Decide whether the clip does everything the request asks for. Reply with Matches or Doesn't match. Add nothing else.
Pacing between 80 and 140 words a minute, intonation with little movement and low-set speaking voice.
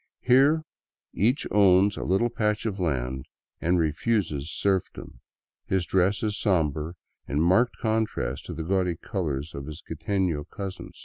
Doesn't match